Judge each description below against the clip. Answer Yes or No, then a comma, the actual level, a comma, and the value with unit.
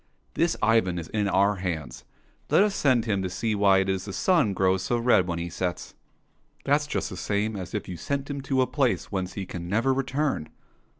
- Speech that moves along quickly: Yes, fast, 235 wpm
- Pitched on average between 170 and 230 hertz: No, low, 100 Hz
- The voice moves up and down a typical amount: No, wide, 6.0 semitones